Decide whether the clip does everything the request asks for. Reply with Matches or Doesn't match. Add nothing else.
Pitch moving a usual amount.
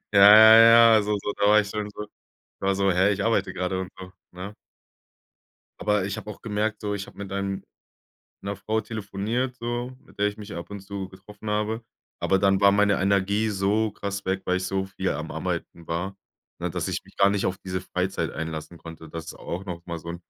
Doesn't match